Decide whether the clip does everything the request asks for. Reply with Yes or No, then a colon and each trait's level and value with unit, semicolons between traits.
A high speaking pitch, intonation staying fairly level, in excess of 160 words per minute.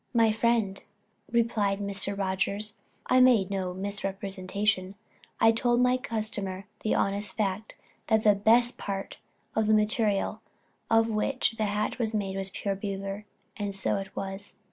No: high, 205 Hz; narrow, 2.3 semitones; average, 145 wpm